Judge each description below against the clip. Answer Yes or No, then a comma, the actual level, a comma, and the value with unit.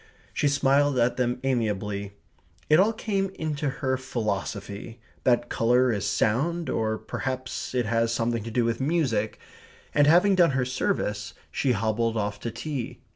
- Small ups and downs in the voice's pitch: No, average, 4.2 semitones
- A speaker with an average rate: Yes, average, 155 wpm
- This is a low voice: Yes, low, 125 Hz